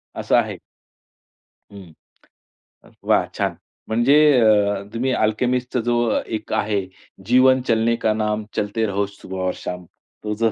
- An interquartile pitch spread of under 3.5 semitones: Yes, narrow, 2.6 semitones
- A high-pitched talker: No, low, 110 Hz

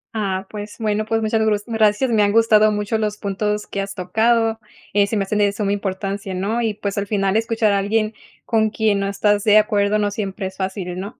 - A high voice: Yes, high, 210 Hz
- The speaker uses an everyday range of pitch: No, narrow, 1.7 semitones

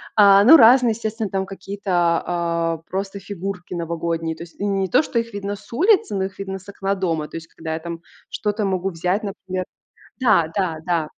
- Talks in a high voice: Yes, high, 195 Hz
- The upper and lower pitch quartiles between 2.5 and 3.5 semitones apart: Yes, average, 3.2 semitones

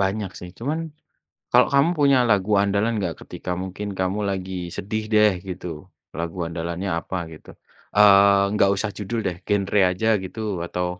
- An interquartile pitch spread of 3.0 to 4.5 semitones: No, narrow, 2.4 semitones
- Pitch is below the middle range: Yes, low, 100 Hz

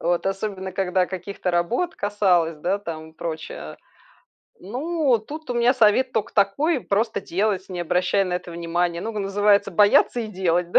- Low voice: No, high, 195 Hz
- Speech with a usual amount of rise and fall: Yes, average, 3.8 semitones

